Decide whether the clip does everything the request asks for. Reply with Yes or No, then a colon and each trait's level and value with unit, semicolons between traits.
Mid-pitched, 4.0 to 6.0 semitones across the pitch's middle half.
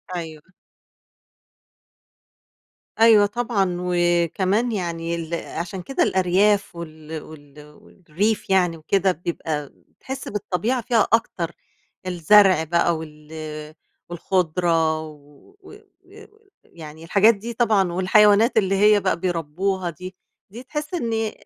Yes: medium, 180 Hz; average, 4.3 semitones